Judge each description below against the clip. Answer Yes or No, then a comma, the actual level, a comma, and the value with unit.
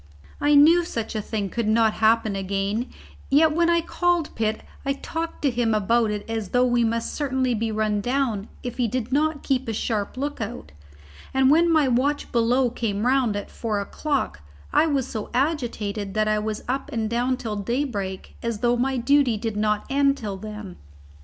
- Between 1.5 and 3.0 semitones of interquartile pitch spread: No, average, 4.2 semitones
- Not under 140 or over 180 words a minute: No, average, 190 wpm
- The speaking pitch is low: No, high, 235 Hz